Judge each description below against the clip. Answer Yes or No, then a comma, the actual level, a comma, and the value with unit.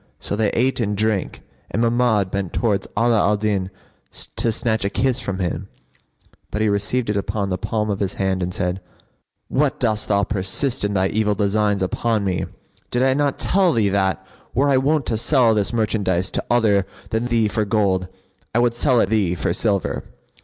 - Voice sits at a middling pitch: No, low, 105 Hz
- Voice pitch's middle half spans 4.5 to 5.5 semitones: No, average, 3.1 semitones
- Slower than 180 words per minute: No, average, 195 wpm